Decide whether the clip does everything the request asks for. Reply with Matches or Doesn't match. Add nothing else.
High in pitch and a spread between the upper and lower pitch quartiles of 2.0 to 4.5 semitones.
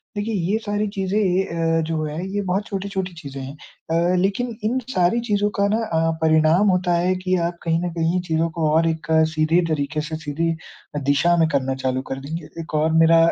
Doesn't match